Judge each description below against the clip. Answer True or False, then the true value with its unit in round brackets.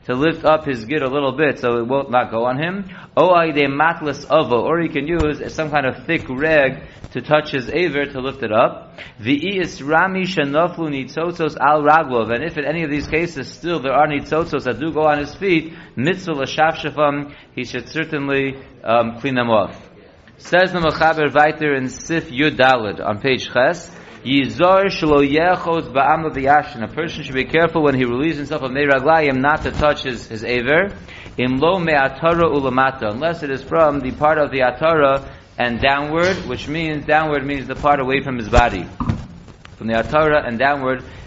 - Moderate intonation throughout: True (3.4 semitones)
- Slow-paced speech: False (200 wpm)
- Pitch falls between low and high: True (145 Hz)